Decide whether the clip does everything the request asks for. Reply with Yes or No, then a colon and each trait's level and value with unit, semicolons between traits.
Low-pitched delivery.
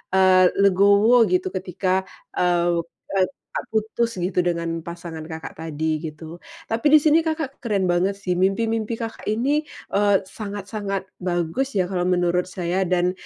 No: high, 190 Hz